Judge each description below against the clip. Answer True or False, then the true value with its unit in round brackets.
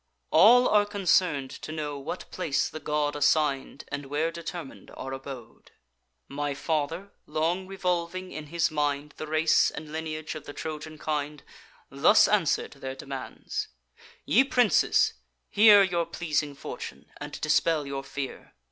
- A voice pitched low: False (155 Hz)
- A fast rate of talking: False (140 wpm)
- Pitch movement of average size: True (3.2 semitones)